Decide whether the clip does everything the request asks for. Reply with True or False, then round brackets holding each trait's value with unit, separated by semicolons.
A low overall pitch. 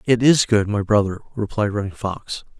True (110 Hz)